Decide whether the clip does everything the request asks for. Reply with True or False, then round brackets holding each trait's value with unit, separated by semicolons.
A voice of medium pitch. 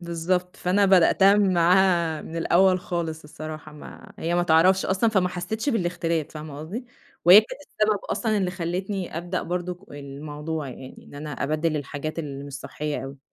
True (170 Hz)